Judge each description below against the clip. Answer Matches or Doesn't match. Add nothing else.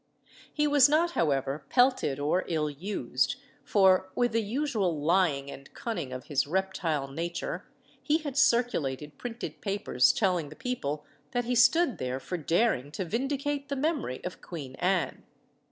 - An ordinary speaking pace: Matches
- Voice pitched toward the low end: Doesn't match